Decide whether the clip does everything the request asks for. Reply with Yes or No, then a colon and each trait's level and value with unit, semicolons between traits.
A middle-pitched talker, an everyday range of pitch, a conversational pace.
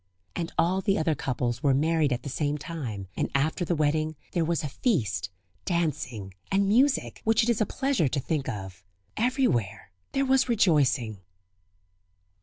No: medium, 155 Hz; wide, 7.7 semitones; average, 165 wpm